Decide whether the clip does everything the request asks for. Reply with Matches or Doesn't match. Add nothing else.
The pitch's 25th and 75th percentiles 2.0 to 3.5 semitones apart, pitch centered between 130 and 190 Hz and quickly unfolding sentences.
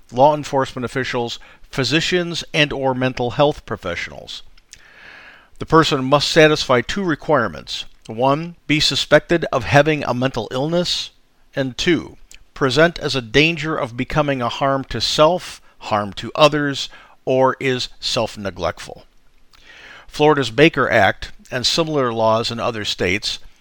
Doesn't match